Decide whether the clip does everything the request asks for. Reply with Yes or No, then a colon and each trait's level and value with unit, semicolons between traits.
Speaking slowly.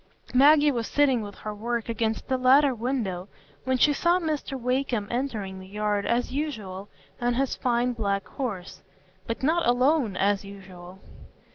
No: average, 155 wpm